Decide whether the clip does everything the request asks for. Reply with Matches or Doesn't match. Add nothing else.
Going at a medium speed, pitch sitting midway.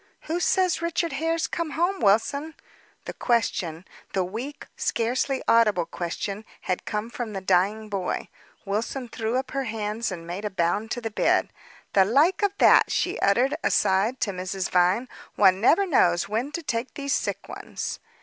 Doesn't match